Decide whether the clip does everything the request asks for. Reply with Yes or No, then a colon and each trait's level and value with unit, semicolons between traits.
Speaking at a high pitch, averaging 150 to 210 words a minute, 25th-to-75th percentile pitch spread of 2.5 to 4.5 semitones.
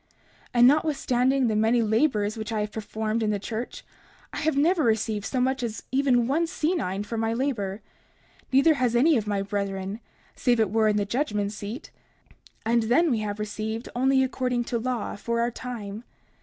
Yes: high, 230 Hz; average, 185 wpm; average, 3.6 semitones